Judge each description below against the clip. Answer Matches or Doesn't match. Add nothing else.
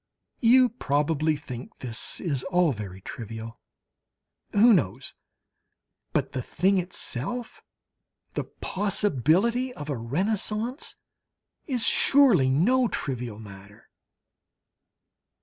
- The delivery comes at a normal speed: Doesn't match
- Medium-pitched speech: Matches